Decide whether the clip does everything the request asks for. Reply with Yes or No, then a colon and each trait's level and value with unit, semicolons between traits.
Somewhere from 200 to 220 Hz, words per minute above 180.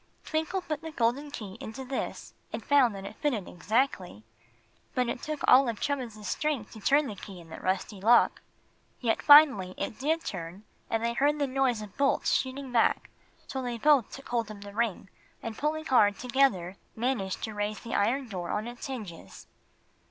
No: high, 235 Hz; average, 190 wpm